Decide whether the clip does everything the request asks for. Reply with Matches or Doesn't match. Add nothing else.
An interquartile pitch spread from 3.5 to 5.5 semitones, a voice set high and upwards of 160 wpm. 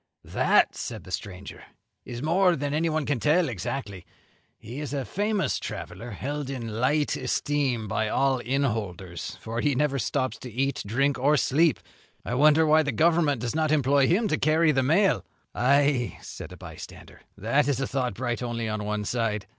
Doesn't match